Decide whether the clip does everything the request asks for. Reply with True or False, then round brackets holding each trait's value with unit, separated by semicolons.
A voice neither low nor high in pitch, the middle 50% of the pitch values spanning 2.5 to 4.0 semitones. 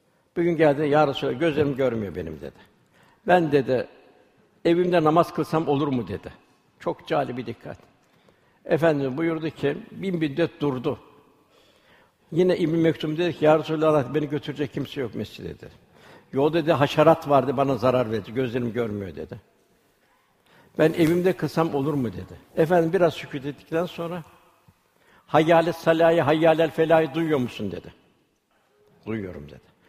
True (155 Hz; 3.2 semitones)